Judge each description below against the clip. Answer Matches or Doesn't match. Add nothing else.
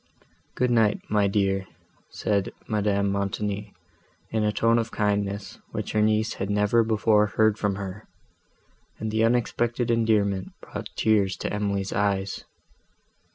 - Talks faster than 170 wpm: Doesn't match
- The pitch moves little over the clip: Matches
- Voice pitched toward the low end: Matches